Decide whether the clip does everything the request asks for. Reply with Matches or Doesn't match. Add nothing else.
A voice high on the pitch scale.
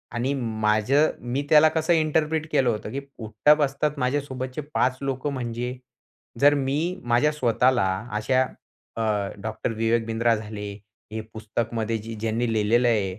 Doesn't match